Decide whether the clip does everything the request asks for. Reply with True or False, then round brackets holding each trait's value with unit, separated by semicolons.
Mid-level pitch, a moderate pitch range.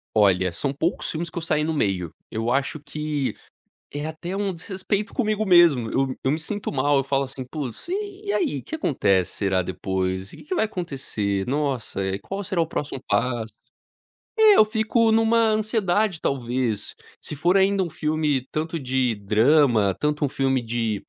False (145 Hz; 8.0 semitones)